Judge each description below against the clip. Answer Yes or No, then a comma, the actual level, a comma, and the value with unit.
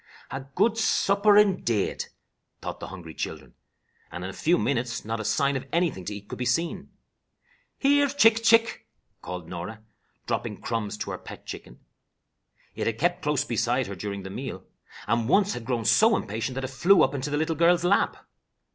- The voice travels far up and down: Yes, wide, 8.6 semitones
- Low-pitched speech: Yes, low, 130 Hz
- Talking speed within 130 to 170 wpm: No, average, 185 wpm